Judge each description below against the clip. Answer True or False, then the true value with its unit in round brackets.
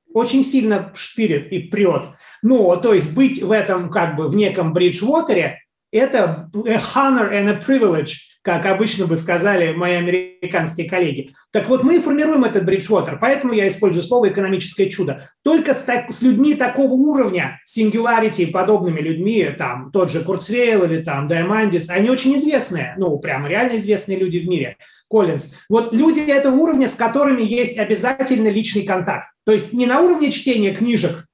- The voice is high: True (210 Hz)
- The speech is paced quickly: True (170 wpm)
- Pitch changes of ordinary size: False (5.7 semitones)